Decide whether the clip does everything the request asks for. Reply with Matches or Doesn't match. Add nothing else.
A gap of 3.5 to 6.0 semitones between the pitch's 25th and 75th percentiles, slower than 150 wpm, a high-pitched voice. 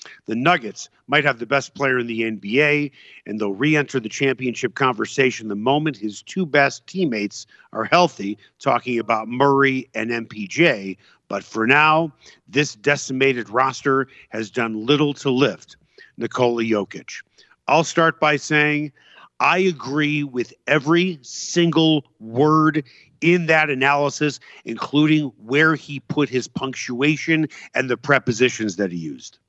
Doesn't match